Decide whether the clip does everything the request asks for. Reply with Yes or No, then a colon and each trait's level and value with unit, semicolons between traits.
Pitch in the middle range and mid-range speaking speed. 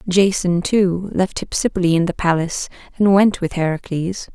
Yes: medium, 180 Hz; average, 150 wpm